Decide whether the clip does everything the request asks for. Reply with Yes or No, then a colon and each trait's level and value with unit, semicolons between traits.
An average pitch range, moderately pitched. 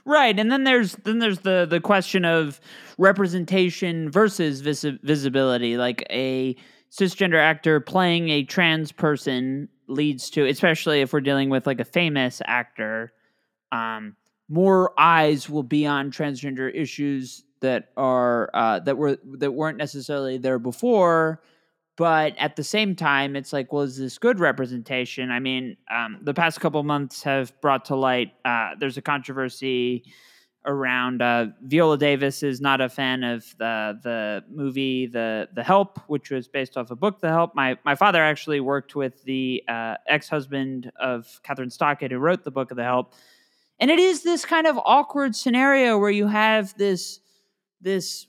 Yes: average, 4.9 semitones; medium, 145 Hz